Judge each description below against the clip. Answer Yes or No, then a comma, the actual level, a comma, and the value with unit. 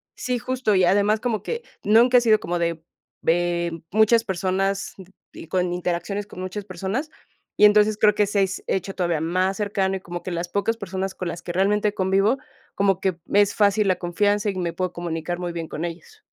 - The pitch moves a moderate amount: Yes, average, 3.1 semitones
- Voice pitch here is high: Yes, high, 195 Hz